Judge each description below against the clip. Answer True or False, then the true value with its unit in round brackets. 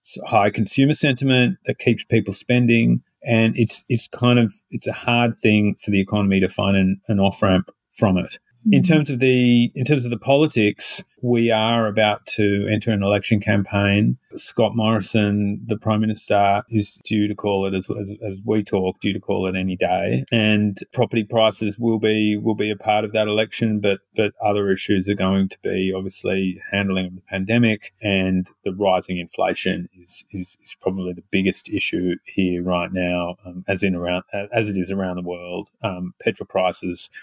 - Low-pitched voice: True (105 Hz)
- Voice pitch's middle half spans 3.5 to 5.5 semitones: False (2.7 semitones)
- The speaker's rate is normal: True (185 wpm)